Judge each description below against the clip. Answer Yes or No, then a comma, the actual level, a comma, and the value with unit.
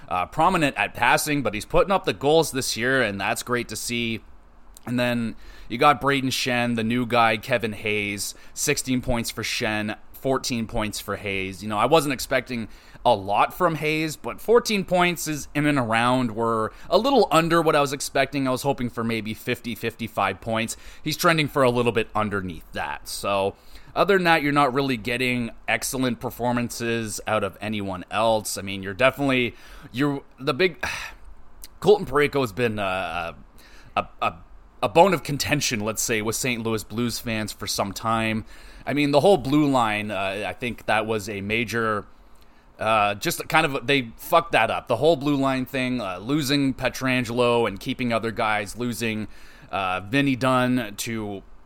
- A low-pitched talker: Yes, low, 120 Hz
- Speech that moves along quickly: No, average, 180 wpm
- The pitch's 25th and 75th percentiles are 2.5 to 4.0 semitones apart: No, average, 4.5 semitones